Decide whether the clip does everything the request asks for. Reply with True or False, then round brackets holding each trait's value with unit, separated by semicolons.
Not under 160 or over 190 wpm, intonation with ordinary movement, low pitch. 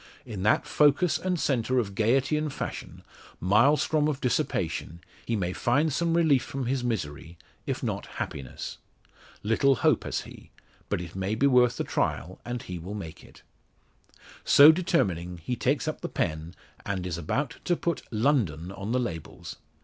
False (165 wpm; 7.6 semitones; 120 Hz)